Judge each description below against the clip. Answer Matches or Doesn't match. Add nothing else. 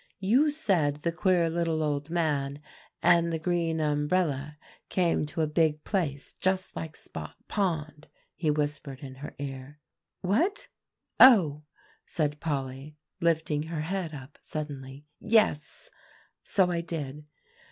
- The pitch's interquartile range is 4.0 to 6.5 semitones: Doesn't match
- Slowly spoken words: Matches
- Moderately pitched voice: Matches